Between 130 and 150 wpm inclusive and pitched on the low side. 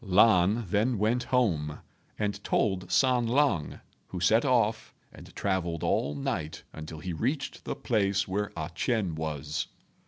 Yes: average, 145 wpm; low, 100 Hz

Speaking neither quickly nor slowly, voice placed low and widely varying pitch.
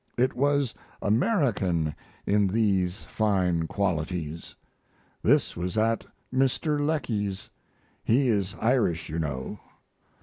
No: slow, 100 wpm; low, 100 Hz; wide, 5.9 semitones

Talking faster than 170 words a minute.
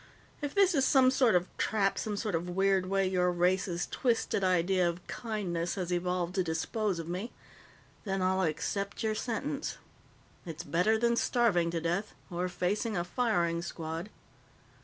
No: average, 160 wpm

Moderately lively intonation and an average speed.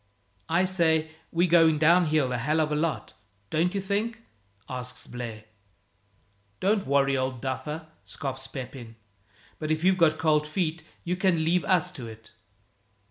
Yes: average, 4.7 semitones; average, 150 wpm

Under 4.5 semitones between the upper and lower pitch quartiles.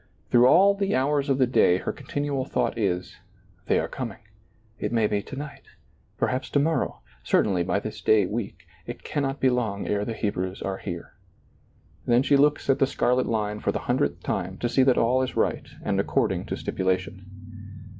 No: average, 5.2 semitones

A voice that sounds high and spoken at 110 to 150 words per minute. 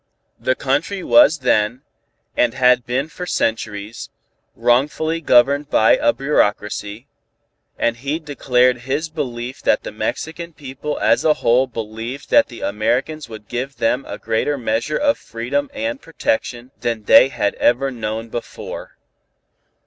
No: low, 130 Hz; average, 140 wpm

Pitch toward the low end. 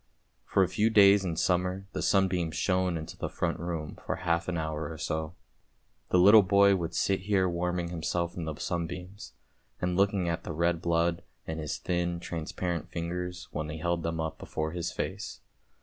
Yes: very low, 85 Hz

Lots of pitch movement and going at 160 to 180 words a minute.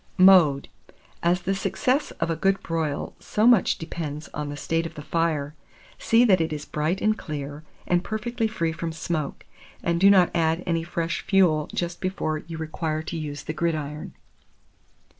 No: average, 3.1 semitones; average, 175 wpm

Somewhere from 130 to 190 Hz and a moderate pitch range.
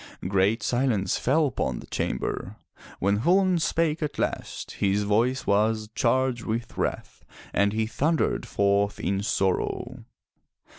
No: low, 110 Hz; average, 4.7 semitones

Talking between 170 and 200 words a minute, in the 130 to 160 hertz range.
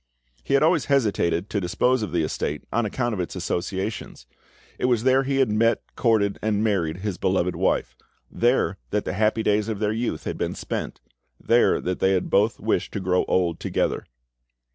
No: average, 185 wpm; low, 105 Hz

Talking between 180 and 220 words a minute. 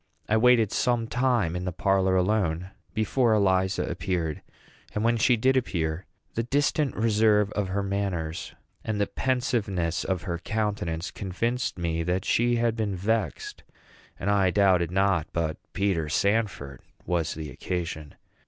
No: average, 145 wpm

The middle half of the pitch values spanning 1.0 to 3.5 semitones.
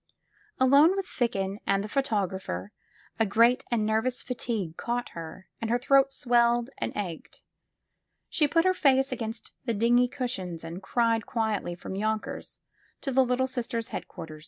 No: average, 4.4 semitones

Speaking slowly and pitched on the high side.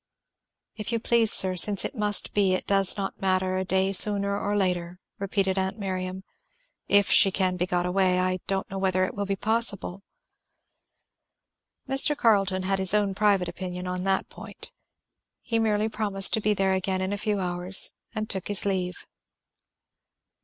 No: average, 175 wpm; high, 195 Hz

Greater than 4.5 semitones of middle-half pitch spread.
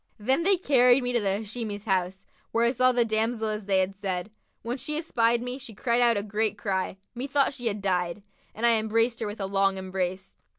No: average, 3.8 semitones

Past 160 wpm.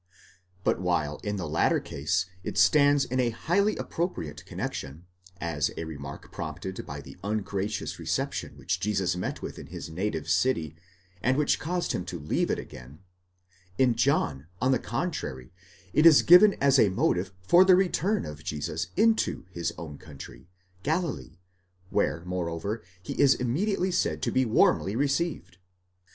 No: average, 155 wpm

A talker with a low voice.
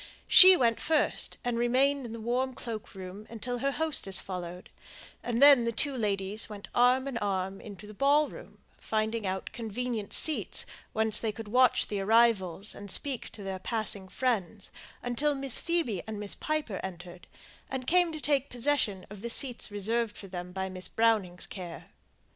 No: high, 225 Hz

